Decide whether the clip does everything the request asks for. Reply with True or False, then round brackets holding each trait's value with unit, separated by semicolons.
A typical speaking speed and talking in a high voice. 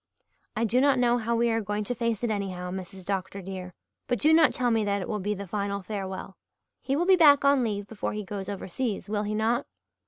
False (240 wpm; 210 Hz)